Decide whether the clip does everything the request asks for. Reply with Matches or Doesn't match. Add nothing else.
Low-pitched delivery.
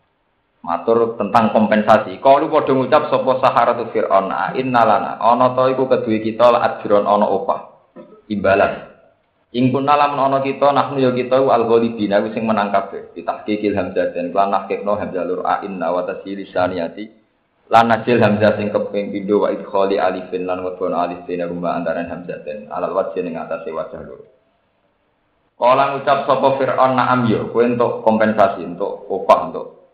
Matches